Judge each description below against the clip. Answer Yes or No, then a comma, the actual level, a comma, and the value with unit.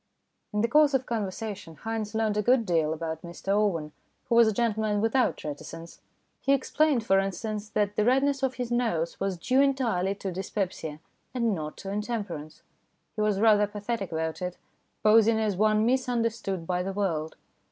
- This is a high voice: Yes, high, 210 Hz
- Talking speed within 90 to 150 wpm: No, average, 175 wpm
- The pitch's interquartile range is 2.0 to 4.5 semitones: Yes, average, 4.1 semitones